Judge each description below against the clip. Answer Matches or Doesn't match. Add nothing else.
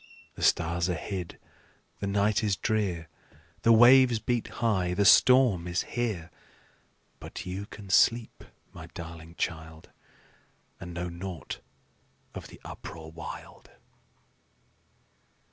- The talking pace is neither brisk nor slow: Doesn't match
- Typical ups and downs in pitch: Matches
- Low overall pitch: Matches